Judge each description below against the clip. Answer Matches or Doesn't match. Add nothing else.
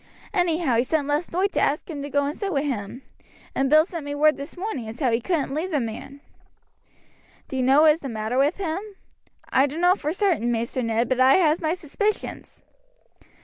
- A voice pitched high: Matches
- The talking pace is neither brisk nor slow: Doesn't match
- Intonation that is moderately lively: Matches